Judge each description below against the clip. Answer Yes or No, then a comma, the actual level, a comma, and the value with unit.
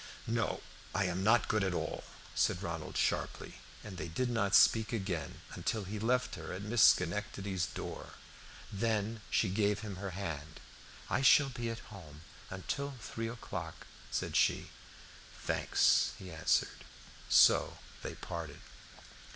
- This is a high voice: No, low, 100 Hz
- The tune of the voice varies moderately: Yes, average, 3.9 semitones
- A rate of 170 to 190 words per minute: No, average, 145 wpm